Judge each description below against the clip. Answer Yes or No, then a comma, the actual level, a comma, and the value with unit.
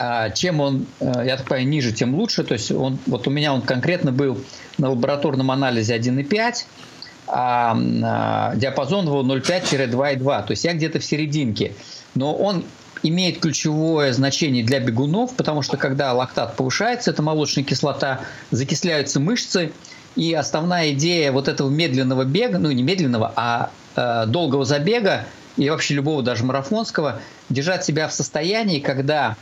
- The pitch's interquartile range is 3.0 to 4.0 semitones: Yes, average, 3.3 semitones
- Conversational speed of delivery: Yes, average, 150 wpm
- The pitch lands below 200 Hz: Yes, medium, 140 Hz